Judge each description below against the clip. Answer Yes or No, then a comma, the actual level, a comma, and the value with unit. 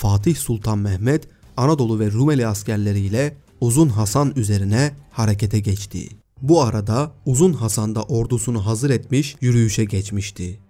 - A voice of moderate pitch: No, low, 115 Hz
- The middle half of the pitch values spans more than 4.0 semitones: Yes, average, 4.7 semitones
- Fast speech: No, average, 125 wpm